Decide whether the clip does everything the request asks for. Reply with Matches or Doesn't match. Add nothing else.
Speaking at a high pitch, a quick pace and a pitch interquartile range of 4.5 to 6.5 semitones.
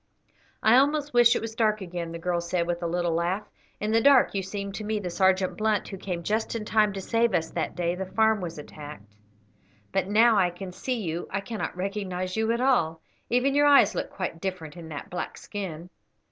Doesn't match